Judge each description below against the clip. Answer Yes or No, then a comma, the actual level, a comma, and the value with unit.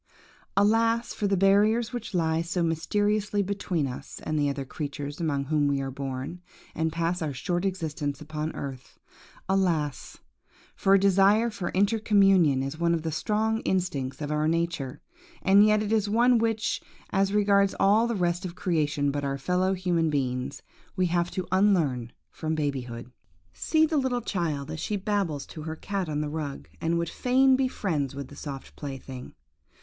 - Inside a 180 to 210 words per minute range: No, average, 170 wpm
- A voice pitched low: No, medium, 170 Hz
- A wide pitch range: Yes, wide, 5.7 semitones